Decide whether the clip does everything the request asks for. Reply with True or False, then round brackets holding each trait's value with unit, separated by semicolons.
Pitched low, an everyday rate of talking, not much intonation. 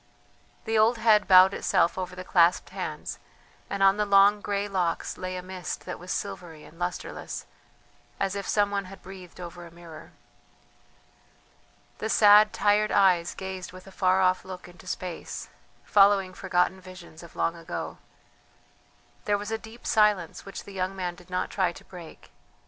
False (185 Hz; 170 wpm; 2.1 semitones)